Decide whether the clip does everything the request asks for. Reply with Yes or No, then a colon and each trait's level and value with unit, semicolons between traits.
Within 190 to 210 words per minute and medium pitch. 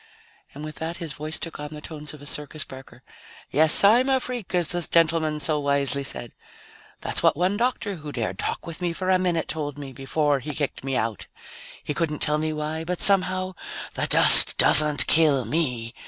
Yes: average, 200 wpm; medium, 155 Hz